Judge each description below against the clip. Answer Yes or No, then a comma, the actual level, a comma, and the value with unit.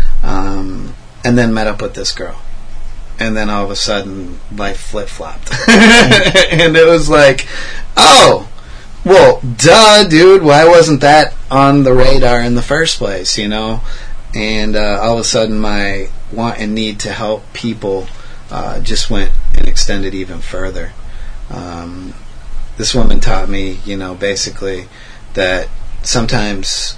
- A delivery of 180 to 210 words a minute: No, average, 150 wpm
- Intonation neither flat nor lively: Yes, average, 4.4 semitones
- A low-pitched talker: Yes, low, 110 Hz